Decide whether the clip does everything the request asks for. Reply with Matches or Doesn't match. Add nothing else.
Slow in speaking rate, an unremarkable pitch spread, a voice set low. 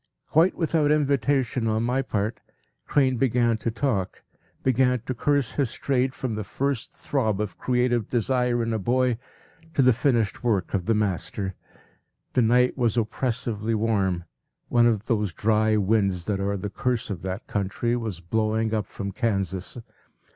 Doesn't match